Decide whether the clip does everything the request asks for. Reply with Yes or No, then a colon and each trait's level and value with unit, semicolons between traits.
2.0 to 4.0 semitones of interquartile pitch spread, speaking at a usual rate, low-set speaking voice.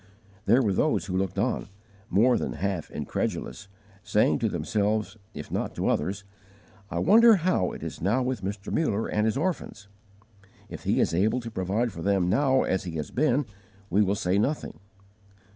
No: average, 4.8 semitones; average, 175 wpm; low, 105 Hz